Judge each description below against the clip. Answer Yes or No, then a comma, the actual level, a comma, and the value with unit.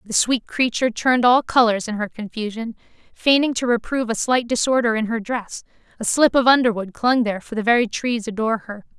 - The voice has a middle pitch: No, high, 230 Hz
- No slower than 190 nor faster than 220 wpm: Yes, average, 200 wpm